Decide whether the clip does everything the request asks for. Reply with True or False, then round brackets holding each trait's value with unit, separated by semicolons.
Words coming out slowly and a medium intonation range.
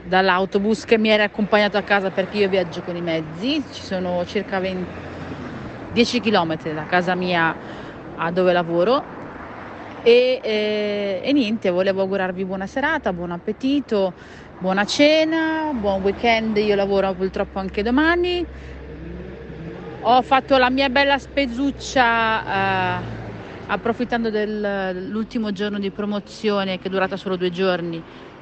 False (135 wpm; 3.8 semitones)